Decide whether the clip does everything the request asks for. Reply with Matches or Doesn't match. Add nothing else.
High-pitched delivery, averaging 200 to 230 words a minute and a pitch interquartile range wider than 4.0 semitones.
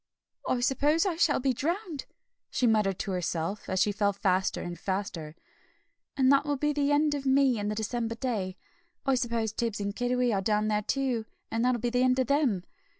Matches